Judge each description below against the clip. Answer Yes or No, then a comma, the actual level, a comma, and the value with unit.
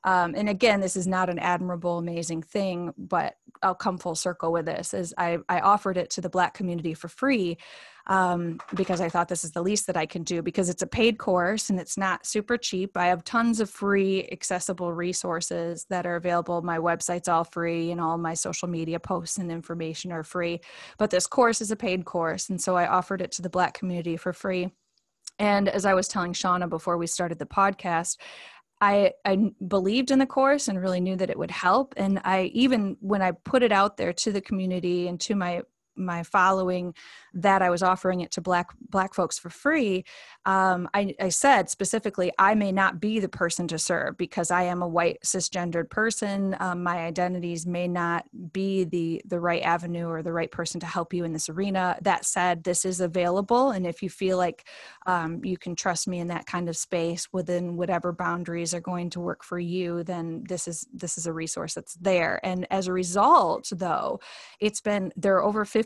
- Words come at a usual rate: No, fast, 210 wpm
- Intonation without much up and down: Yes, narrow, 2.1 semitones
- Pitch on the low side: No, medium, 180 Hz